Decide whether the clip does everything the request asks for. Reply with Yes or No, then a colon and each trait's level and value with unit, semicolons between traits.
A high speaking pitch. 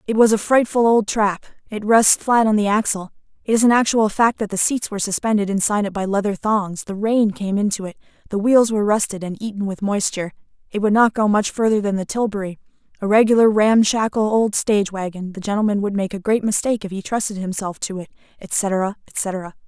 Yes: high, 205 Hz